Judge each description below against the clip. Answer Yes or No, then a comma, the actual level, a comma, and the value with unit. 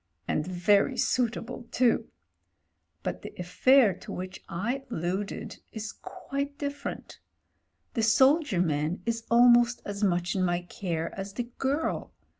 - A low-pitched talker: No, high, 215 Hz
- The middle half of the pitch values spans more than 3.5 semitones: Yes, wide, 5.6 semitones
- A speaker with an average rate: No, slow, 130 wpm